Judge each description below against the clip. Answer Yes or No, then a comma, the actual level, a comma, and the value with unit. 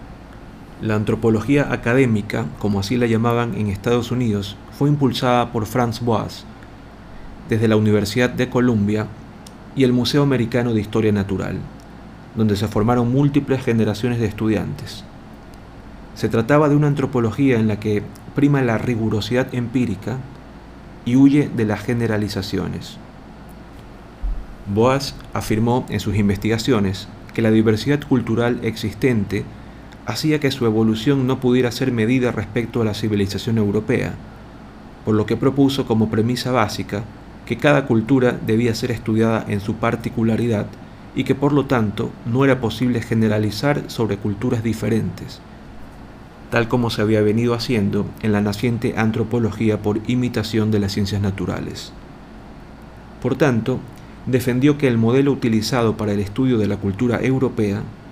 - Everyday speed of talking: Yes, average, 135 wpm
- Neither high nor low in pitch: No, low, 115 Hz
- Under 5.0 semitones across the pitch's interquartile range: Yes, average, 2.9 semitones